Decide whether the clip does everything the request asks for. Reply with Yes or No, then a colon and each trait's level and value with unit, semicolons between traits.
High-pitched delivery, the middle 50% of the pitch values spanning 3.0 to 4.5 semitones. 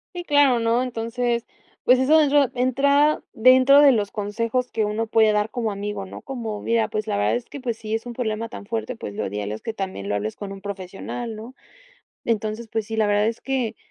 Yes: high, 225 Hz; average, 3.3 semitones